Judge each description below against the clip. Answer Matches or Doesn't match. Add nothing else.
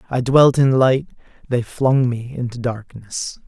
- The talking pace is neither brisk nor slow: Matches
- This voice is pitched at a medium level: Doesn't match